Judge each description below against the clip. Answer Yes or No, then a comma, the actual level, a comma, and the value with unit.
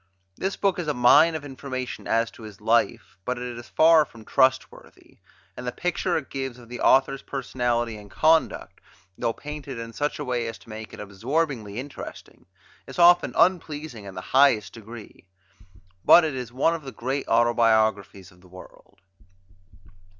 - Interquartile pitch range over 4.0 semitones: Yes, average, 4.5 semitones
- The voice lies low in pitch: Yes, low, 125 Hz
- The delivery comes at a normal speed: Yes, average, 170 wpm